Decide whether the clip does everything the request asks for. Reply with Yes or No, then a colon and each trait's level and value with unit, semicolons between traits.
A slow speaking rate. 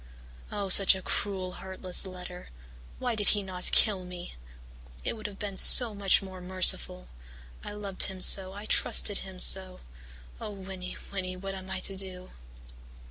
No: average, 165 wpm